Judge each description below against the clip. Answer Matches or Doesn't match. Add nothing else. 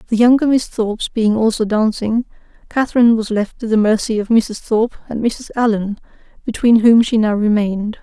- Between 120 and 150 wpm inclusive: Doesn't match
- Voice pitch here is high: Matches